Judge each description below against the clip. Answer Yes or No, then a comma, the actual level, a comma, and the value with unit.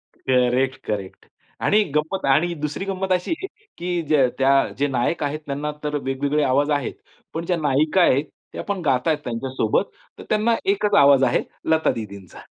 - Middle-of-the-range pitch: Yes, medium, 145 Hz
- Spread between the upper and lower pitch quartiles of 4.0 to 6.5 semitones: Yes, average, 4.7 semitones